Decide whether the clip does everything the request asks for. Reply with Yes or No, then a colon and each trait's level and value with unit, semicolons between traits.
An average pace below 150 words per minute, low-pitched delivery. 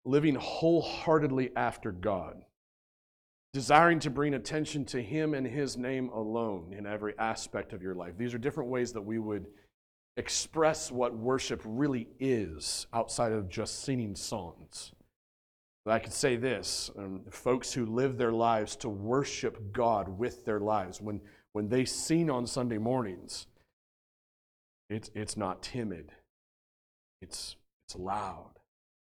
Yes: average, 140 wpm; low, 115 Hz